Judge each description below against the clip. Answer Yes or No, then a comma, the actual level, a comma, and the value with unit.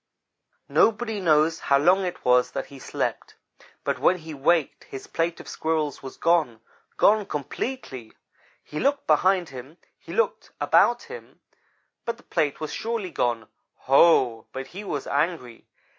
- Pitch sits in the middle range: Yes, medium, 160 Hz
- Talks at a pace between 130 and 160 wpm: Yes, average, 150 wpm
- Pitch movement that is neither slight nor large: No, wide, 6.0 semitones